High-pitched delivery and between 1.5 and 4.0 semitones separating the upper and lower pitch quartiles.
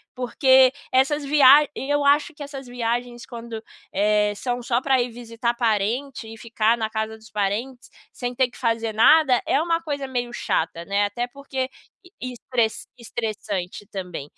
Yes: high, 240 Hz; average, 3.3 semitones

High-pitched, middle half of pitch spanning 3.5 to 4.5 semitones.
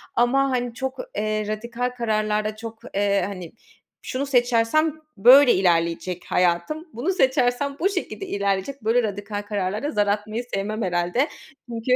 Yes: high, 220 Hz; average, 4.1 semitones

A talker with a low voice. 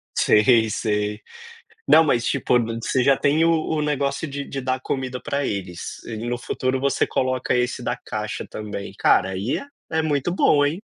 Yes: low, 130 Hz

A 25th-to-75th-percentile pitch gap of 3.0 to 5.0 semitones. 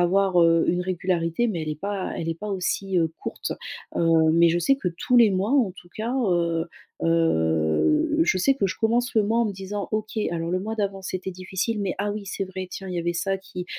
Yes: average, 3.7 semitones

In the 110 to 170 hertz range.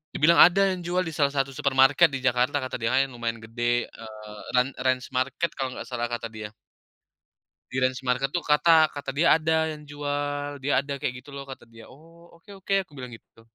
Yes: low, 135 Hz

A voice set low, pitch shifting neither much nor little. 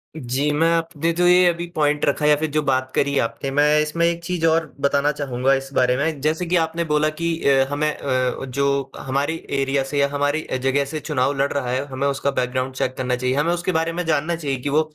No: medium, 145 Hz; average, 3.0 semitones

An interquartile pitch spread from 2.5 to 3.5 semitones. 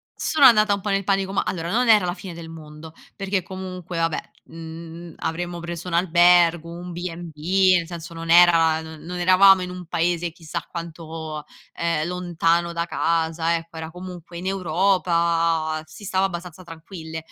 No: narrow, 1.8 semitones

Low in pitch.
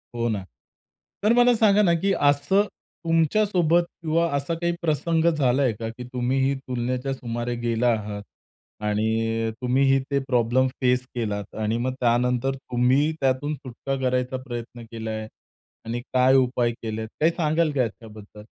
Yes: low, 125 Hz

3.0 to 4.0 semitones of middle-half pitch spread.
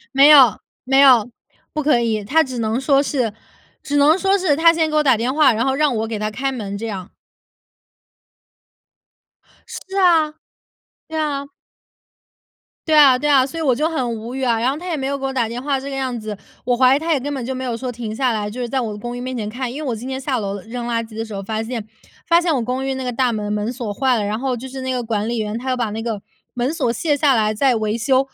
Yes: average, 3.7 semitones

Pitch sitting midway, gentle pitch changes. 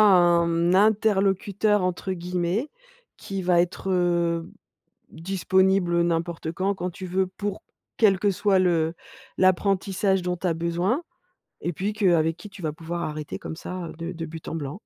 Yes: medium, 180 Hz; narrow, 2.3 semitones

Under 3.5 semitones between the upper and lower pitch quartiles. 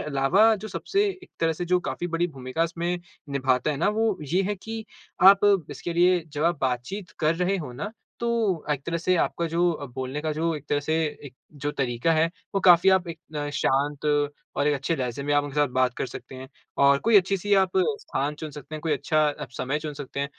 No: average, 4.3 semitones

